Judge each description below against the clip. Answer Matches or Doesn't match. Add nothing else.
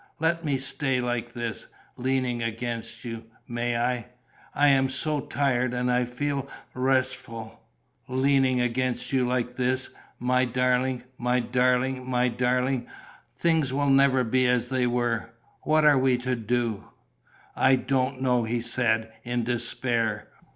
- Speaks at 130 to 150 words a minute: Matches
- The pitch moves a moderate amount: Doesn't match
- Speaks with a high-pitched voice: Doesn't match